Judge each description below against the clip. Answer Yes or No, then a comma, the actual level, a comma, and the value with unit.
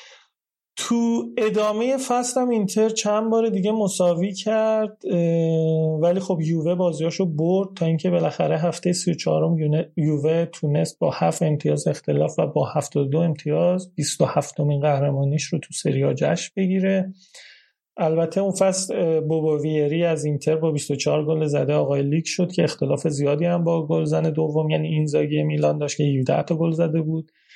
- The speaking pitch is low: No, medium, 165 Hz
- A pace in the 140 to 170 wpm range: Yes, fast, 155 wpm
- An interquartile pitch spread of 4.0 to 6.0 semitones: No, average, 3.6 semitones